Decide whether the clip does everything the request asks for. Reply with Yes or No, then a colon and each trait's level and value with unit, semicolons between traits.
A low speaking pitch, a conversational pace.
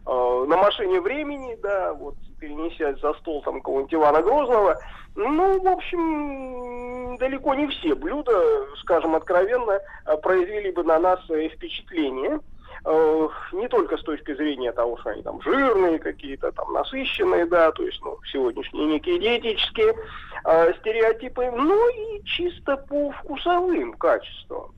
No: very high, 250 Hz; average, 135 wpm